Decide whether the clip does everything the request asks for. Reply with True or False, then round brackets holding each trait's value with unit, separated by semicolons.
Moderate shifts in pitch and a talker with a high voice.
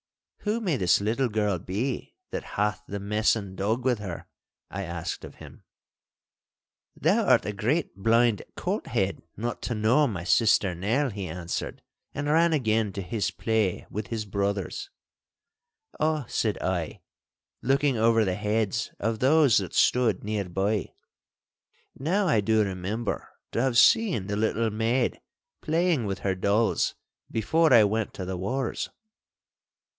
False (4.1 semitones; 110 Hz)